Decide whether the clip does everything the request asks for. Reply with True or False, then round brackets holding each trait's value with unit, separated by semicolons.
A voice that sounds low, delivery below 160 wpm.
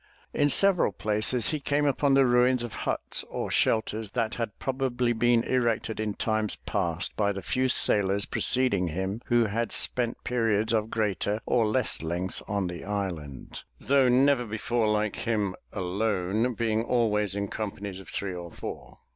False (110 Hz; 165 wpm)